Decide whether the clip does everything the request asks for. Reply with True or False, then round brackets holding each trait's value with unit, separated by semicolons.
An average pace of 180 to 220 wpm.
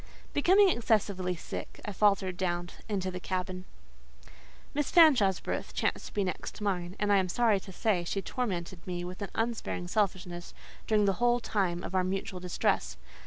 False (170 wpm)